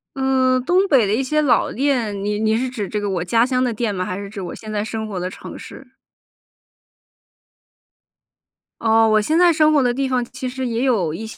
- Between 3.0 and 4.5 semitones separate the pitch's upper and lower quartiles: Yes, average, 3.9 semitones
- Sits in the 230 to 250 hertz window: Yes, high, 235 Hz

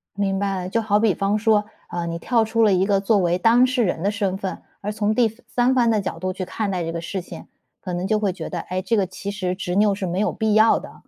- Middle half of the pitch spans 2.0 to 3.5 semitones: Yes, average, 2.8 semitones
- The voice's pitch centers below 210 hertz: Yes, high, 200 Hz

